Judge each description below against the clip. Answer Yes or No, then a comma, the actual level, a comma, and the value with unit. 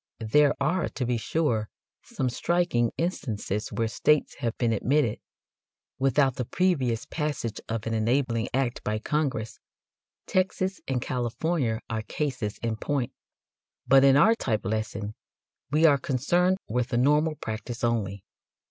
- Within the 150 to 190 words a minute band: No, average, 140 wpm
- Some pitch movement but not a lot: Yes, average, 4.7 semitones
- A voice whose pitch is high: No, low, 125 Hz